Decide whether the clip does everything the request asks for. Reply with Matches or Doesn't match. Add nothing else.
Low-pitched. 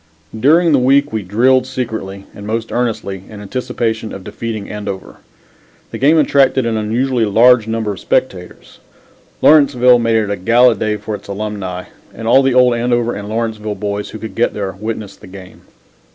Matches